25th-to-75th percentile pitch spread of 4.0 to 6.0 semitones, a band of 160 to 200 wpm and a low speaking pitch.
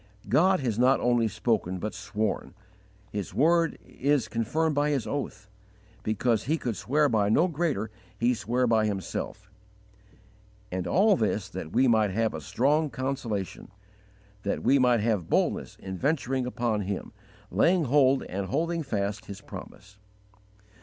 No: wide, 5.4 semitones; average, 150 wpm; low, 120 Hz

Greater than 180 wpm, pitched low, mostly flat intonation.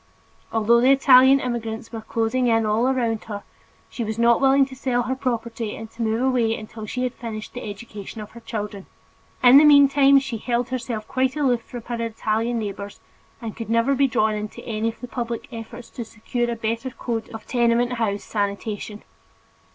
No: average, 190 wpm; high, 230 Hz; narrow, 2.3 semitones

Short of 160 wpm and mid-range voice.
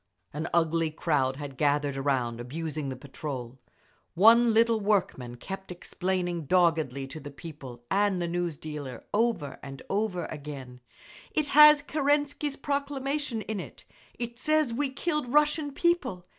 Yes: average, 140 wpm; medium, 175 Hz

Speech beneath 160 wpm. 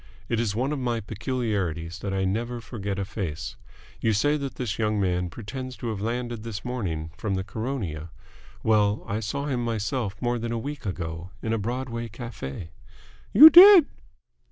No: average, 180 wpm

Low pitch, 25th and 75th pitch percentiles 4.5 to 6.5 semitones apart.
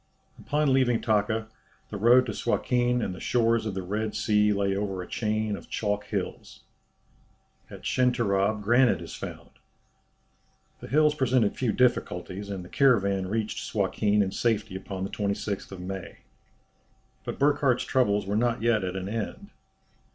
No: low, 110 Hz; average, 3.6 semitones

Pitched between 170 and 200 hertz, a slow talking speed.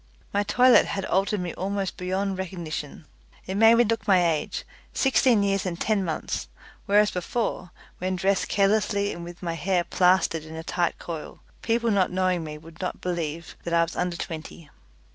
No: medium, 185 Hz; average, 180 wpm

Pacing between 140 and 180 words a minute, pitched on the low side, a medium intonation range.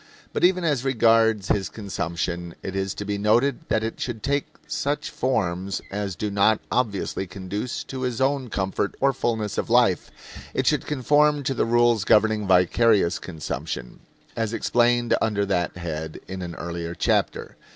Yes: average, 160 wpm; low, 105 Hz; average, 4.5 semitones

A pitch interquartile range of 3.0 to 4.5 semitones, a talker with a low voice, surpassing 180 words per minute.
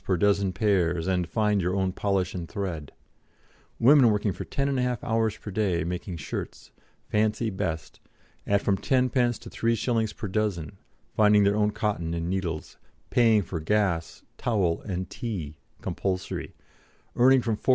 No: average, 3.7 semitones; low, 100 Hz; average, 150 wpm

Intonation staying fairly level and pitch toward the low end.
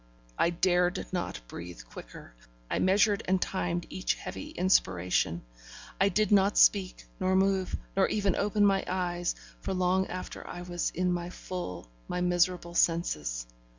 No: narrow, 1.8 semitones; medium, 180 Hz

